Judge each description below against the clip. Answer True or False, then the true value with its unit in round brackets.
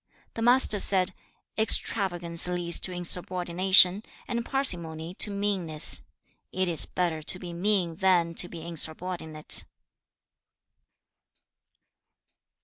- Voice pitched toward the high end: False (180 Hz)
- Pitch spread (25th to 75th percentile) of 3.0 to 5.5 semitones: False (2.4 semitones)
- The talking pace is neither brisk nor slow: False (100 wpm)